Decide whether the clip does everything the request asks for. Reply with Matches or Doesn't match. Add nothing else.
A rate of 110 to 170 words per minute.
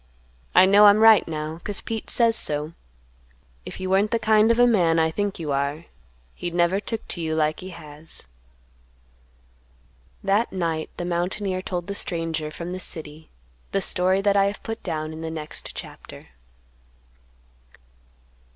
Matches